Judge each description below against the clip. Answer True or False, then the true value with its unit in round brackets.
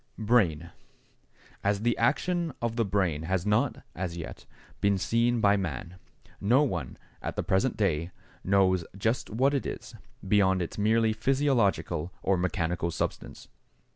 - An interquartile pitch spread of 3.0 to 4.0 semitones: False (4.6 semitones)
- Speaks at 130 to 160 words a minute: True (140 wpm)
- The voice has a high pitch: False (100 Hz)